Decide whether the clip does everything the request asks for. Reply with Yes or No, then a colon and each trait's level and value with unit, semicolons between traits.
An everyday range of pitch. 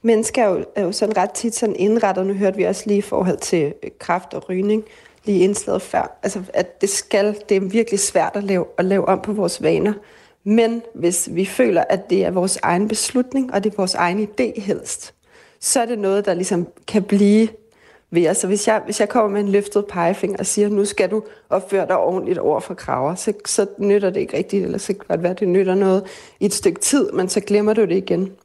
No: narrow, 2.2 semitones